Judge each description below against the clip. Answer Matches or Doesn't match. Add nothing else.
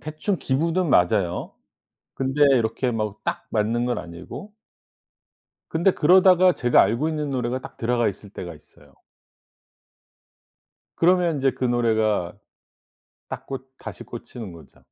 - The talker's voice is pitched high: Doesn't match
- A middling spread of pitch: Doesn't match